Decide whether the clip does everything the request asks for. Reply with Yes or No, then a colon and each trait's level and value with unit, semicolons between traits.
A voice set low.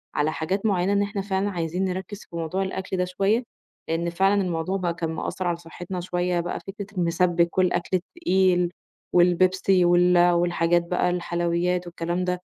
No: medium, 180 Hz